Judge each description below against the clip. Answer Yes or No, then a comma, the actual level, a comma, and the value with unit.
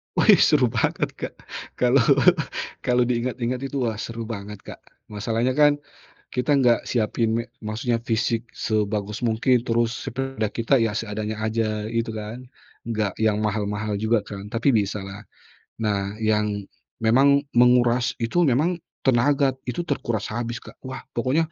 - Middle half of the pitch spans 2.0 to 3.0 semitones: Yes, narrow, 2.6 semitones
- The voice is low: Yes, low, 115 Hz